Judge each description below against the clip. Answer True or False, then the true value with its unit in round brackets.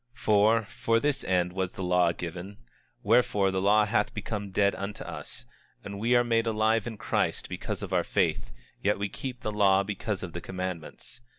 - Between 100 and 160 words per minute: False (195 wpm)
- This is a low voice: True (100 Hz)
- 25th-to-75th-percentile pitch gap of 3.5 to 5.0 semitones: False (2.9 semitones)